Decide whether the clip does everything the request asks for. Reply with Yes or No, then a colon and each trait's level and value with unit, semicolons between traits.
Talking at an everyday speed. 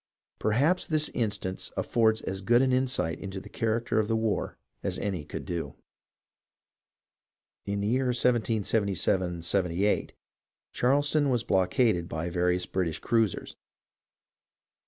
No: slow, 125 wpm